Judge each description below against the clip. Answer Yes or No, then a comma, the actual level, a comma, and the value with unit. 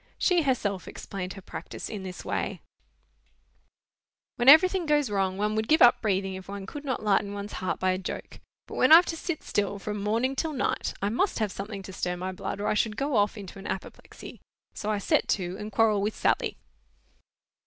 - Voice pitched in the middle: No, high, 210 Hz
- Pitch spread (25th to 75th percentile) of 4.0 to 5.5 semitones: Yes, average, 4.7 semitones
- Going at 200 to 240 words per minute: Yes, fast, 205 wpm